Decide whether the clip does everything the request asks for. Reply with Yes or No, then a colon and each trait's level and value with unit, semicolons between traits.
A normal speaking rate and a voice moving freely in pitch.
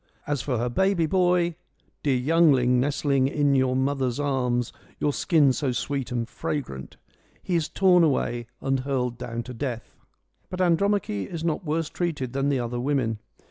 No: average, 170 wpm; average, 4.5 semitones